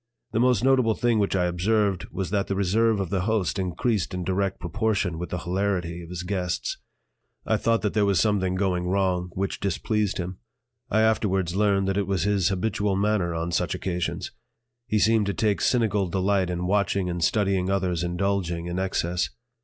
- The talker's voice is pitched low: Yes, very low, 95 Hz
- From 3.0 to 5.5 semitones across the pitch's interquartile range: No, narrow, 2.5 semitones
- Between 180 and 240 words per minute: Yes, average, 185 wpm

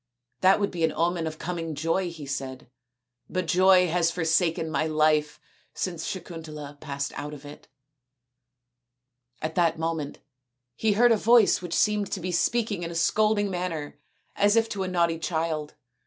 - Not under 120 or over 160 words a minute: No, average, 170 wpm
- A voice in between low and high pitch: Yes, medium, 165 Hz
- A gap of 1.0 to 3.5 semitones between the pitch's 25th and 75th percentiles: Yes, average, 3.2 semitones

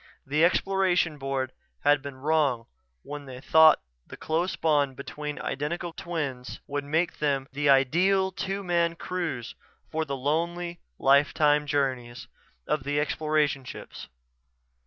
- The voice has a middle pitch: Yes, medium, 150 Hz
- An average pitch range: Yes, average, 3.5 semitones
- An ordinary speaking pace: No, slow, 130 wpm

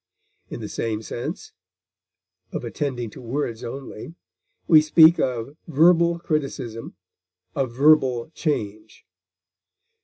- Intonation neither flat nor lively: Yes, average, 4.9 semitones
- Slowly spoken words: Yes, slow, 100 wpm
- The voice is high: No, low, 135 Hz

